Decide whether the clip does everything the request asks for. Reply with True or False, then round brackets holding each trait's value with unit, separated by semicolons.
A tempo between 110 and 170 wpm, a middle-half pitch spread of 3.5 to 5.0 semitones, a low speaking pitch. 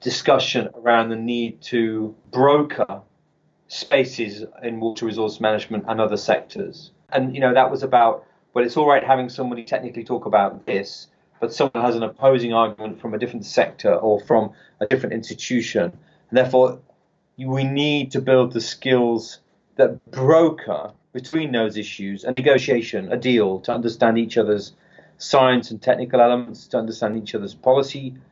False (160 wpm; 2.6 semitones; 120 Hz)